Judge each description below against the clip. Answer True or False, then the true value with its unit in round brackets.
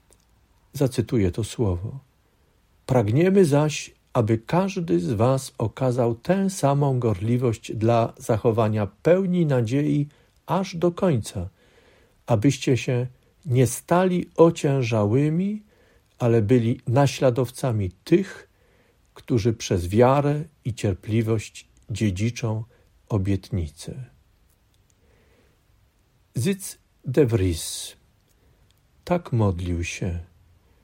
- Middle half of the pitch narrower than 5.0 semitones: False (5.5 semitones)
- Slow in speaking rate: True (80 wpm)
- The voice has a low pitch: True (120 Hz)